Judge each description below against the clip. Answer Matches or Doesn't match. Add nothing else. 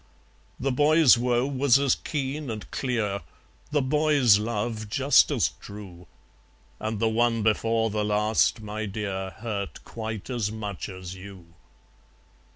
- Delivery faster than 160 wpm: Doesn't match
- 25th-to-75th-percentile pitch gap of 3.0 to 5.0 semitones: Matches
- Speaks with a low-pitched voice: Matches